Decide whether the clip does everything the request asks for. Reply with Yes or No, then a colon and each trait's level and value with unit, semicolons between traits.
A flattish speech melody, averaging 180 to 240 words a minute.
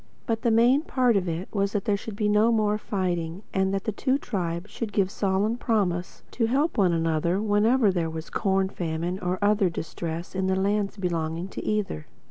No: average, 3.4 semitones; fast, 205 wpm